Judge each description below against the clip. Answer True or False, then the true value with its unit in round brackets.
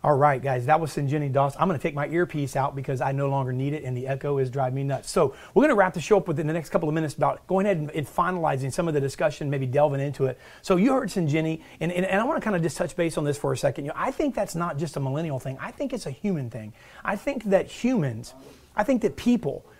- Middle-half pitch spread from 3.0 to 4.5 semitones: False (5.1 semitones)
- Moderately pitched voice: True (155 Hz)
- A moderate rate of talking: False (295 wpm)